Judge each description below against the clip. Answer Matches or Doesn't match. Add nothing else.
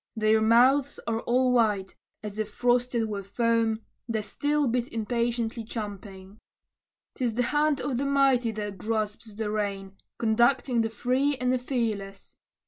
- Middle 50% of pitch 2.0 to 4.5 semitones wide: Matches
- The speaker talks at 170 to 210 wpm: Doesn't match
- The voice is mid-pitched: Doesn't match